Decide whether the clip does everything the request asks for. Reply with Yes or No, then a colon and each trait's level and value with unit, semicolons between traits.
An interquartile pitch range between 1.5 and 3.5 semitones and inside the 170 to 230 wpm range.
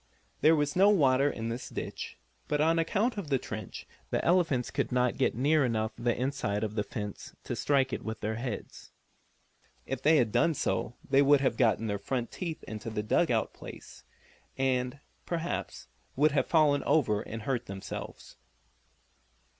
No: average, 4.9 semitones; average, 175 wpm